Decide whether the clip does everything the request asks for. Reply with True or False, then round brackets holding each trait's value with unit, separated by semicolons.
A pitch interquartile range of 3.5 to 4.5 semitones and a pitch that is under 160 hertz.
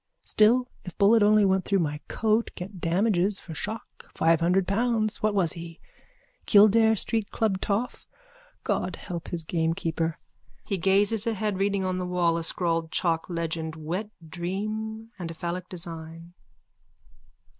False (4.1 semitones; 185 Hz)